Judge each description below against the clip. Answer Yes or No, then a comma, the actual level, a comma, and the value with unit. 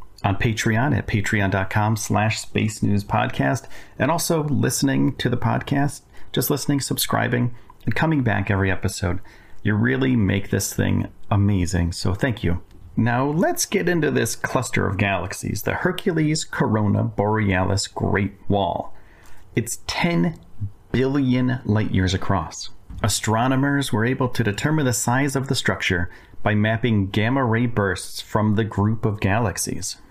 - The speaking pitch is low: Yes, low, 110 Hz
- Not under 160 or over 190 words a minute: No, slow, 135 wpm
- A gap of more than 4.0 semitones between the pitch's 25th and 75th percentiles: Yes, average, 4.6 semitones